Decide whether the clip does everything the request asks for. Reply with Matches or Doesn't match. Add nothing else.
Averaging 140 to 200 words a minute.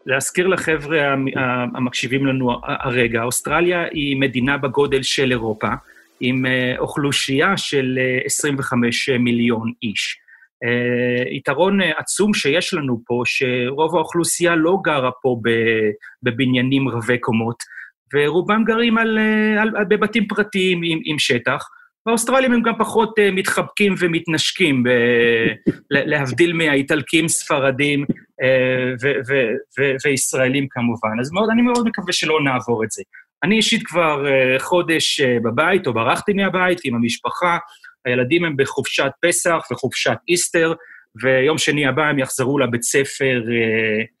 Doesn't match